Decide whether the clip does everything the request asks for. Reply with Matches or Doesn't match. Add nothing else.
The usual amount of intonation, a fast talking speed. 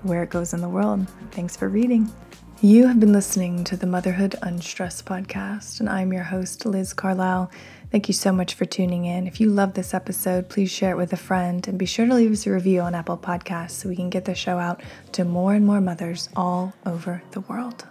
Doesn't match